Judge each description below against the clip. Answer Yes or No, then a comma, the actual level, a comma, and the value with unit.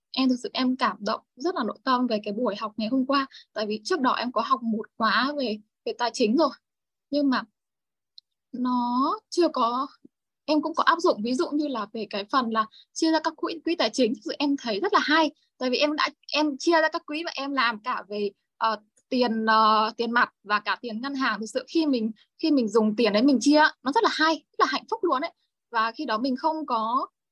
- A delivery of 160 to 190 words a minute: No, fast, 250 wpm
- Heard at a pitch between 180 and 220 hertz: No, very high, 260 Hz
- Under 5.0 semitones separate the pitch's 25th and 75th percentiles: No, wide, 5.5 semitones